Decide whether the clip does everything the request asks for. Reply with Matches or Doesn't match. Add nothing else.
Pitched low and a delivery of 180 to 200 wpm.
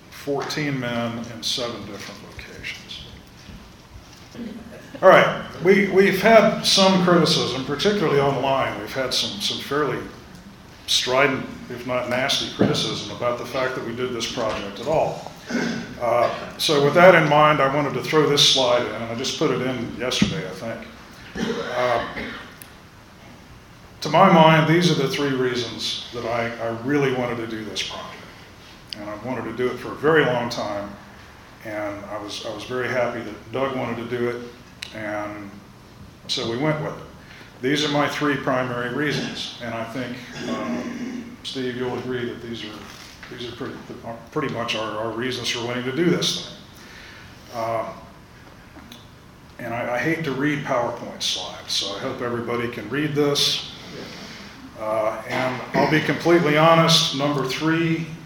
Doesn't match